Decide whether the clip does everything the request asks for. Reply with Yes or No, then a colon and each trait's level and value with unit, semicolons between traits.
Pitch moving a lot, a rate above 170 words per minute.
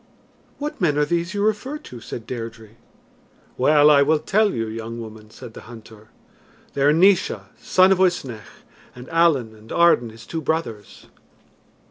No: wide, 7.2 semitones; average, 160 wpm